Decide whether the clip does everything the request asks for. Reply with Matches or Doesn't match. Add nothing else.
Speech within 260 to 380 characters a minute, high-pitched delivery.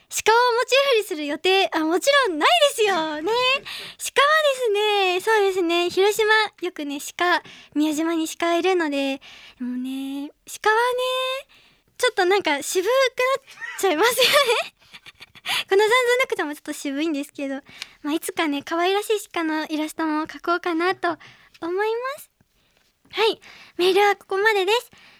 Matches